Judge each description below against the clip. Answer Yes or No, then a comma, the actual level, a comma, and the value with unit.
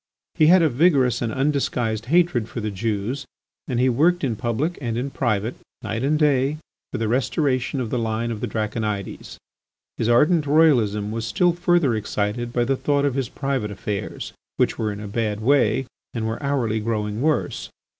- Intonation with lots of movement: No, average, 4.5 semitones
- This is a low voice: Yes, low, 120 Hz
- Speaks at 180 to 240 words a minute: Yes, average, 185 wpm